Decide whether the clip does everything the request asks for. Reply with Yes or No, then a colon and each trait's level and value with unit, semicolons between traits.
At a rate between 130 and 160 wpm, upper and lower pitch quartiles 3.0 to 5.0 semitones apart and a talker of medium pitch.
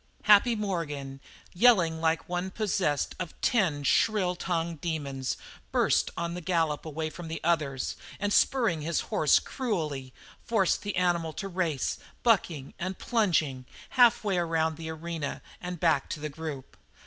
Yes: average, 150 wpm; average, 3.6 semitones; medium, 170 Hz